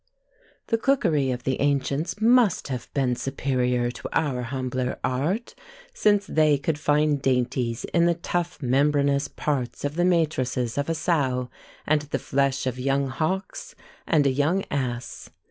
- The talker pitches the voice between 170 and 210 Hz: No, medium, 140 Hz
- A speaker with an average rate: Yes, average, 150 wpm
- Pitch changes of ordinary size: Yes, average, 3.9 semitones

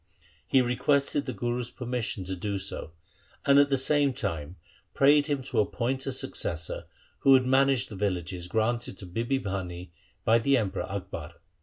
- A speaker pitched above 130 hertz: No, low, 120 Hz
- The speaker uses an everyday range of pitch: No, wide, 5.9 semitones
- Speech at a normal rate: Yes, average, 165 wpm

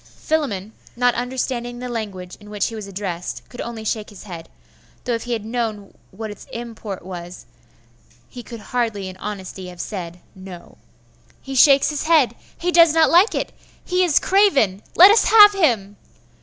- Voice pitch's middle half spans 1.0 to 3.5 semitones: No, wide, 5.6 semitones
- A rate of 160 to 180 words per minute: Yes, average, 175 wpm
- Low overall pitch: No, high, 225 Hz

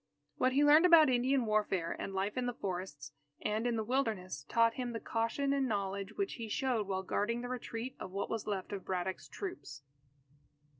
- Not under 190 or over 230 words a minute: Yes, average, 195 wpm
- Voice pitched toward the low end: No, high, 225 Hz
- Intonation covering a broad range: No, average, 4.8 semitones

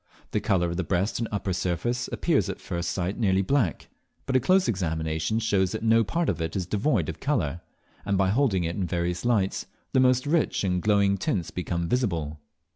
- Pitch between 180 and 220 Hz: No, very low, 95 Hz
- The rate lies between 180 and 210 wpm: Yes, average, 200 wpm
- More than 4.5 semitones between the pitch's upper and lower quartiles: Yes, average, 4.9 semitones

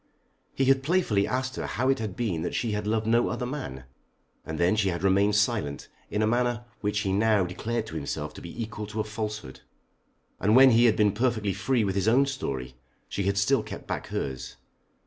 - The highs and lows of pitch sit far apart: No, average, 3.7 semitones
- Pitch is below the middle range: Yes, low, 105 Hz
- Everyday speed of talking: No, fast, 215 wpm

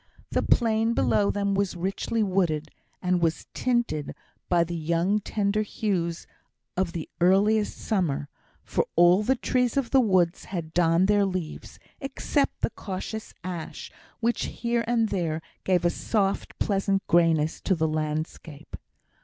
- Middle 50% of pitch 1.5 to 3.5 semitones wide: No, average, 4.2 semitones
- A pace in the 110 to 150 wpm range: Yes, average, 145 wpm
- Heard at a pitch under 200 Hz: Yes, high, 190 Hz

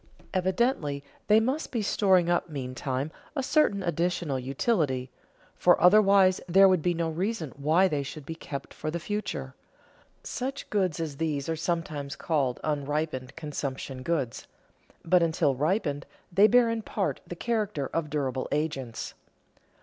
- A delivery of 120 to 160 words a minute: Yes, average, 145 wpm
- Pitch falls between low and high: Yes, medium, 165 Hz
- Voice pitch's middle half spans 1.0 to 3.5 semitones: No, wide, 5.4 semitones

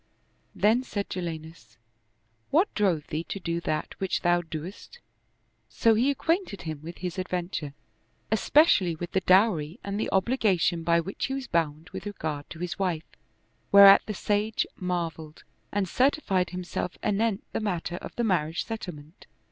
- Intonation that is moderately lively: Yes, average, 4.1 semitones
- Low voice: No, medium, 180 Hz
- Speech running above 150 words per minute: Yes, average, 160 wpm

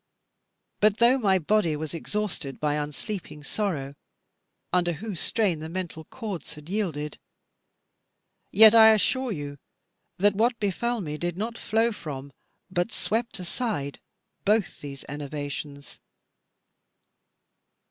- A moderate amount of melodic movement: No, wide, 6.3 semitones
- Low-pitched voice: No, medium, 180 Hz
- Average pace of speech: No, slow, 115 wpm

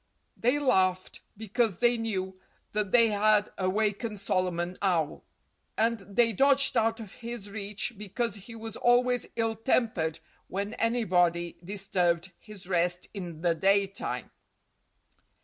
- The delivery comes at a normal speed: No, slow, 125 wpm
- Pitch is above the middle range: Yes, high, 205 Hz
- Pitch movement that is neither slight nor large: Yes, average, 3.6 semitones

